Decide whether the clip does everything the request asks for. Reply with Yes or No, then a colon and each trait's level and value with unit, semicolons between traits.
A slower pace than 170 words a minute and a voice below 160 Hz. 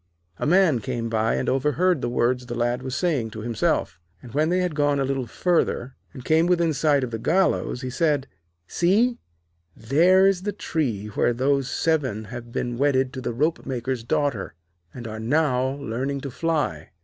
No: average, 185 wpm; low, 135 Hz